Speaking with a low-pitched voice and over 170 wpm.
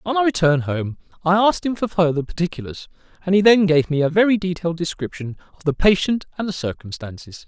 No: medium, 175 Hz; average, 200 wpm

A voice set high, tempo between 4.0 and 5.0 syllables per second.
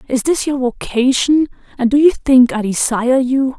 Yes: very high, 260 Hz; 4.8 syllables/s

